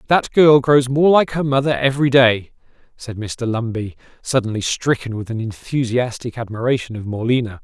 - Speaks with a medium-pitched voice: No, low, 125 Hz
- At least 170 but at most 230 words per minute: No, average, 155 wpm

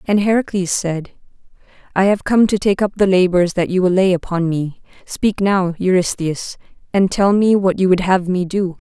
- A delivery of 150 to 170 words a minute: No, average, 195 wpm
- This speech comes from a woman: Yes, female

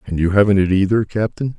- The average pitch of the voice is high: No, low, 100 Hz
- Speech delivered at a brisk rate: Yes, fast, 230 wpm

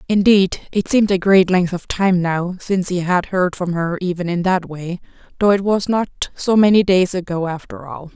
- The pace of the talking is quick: Yes, fast, 215 wpm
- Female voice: Yes, female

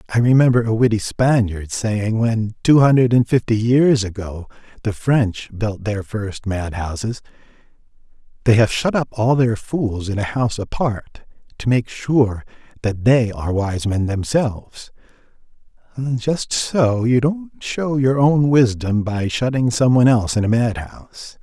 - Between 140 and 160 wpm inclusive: Yes, average, 155 wpm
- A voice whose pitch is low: Yes, low, 115 Hz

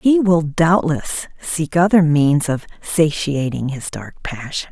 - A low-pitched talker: No, medium, 160 Hz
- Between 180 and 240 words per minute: No, average, 140 wpm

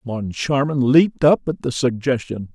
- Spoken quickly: No, average, 140 wpm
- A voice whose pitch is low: Yes, low, 130 Hz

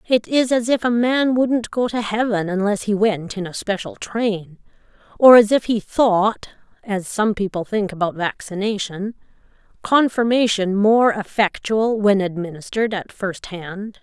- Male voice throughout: No, female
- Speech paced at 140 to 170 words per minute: Yes, average, 155 wpm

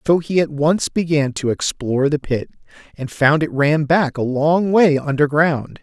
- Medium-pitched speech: Yes, medium, 150 Hz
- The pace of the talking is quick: No, average, 185 wpm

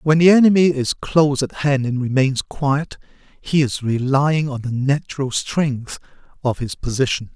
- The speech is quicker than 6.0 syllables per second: No, 4.5 syllables/s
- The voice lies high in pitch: No, medium, 140 Hz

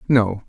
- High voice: No, low, 110 Hz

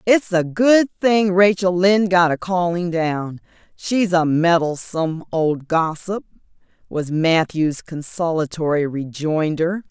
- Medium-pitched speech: Yes, medium, 170 Hz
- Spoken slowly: Yes, slow, 115 wpm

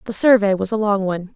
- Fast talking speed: Yes, fast, 265 wpm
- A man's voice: No, female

